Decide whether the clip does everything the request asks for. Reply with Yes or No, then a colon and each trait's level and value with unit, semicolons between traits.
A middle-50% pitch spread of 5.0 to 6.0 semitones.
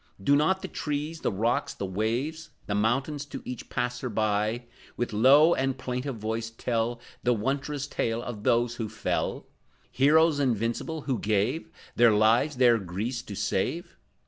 No: average, 4.2 semitones